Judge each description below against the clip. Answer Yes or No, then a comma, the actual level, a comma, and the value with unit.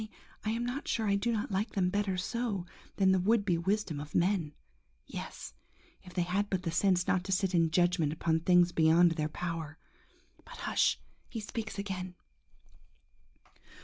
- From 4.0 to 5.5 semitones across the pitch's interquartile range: No, average, 3.1 semitones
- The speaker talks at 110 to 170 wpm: No, average, 180 wpm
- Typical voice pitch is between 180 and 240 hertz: Yes, medium, 185 Hz